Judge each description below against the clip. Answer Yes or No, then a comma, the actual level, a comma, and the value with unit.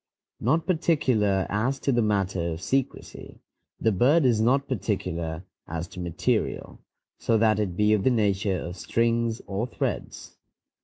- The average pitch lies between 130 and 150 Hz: No, low, 110 Hz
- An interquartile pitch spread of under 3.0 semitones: No, average, 4.6 semitones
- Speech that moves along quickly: No, average, 150 wpm